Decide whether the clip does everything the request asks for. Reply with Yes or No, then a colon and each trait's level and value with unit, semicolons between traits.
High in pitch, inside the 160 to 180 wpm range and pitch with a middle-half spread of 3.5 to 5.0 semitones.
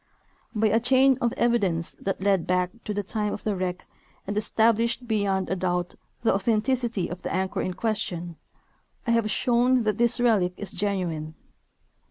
Yes: high, 205 Hz; average, 170 wpm; average, 4.0 semitones